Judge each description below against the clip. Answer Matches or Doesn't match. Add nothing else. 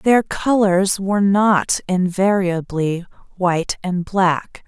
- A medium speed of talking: Doesn't match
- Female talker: Matches